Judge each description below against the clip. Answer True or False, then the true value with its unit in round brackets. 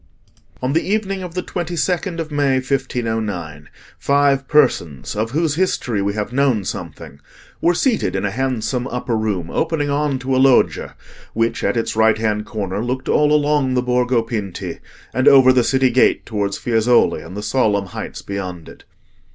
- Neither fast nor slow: True (170 wpm)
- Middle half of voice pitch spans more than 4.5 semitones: True (5.0 semitones)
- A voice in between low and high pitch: False (125 Hz)